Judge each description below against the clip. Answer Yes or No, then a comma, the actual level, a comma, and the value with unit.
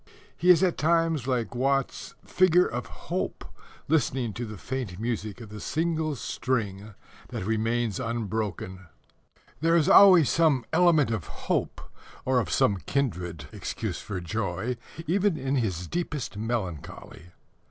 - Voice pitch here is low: Yes, low, 120 Hz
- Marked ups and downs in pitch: Yes, wide, 6.8 semitones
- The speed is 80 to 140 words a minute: Yes, slow, 135 wpm